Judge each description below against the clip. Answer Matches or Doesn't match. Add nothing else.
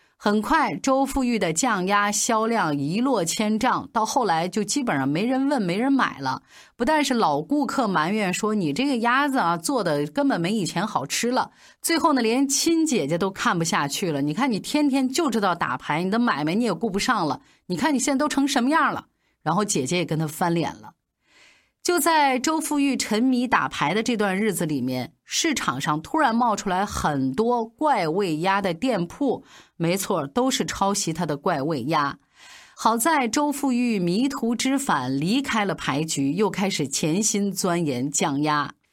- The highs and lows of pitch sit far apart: Matches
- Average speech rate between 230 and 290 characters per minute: Matches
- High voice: Matches